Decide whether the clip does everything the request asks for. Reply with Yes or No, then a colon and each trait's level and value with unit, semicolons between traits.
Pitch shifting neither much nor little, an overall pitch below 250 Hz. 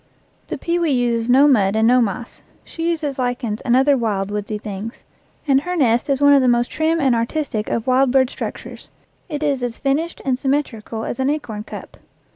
No: average, 3.8 semitones; very high, 255 Hz